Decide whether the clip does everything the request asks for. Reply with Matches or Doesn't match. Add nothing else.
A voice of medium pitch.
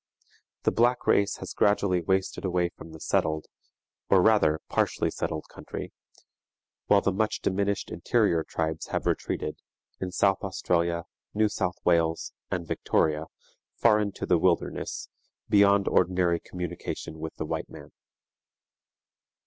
Doesn't match